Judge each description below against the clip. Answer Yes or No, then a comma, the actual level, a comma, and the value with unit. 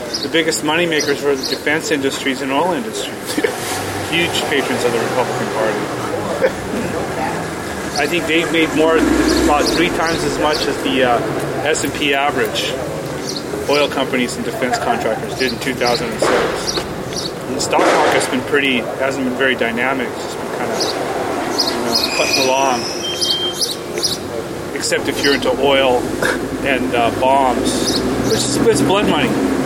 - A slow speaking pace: No, average, 145 wpm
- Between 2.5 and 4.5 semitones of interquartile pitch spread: Yes, average, 3.6 semitones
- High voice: No, medium, 140 Hz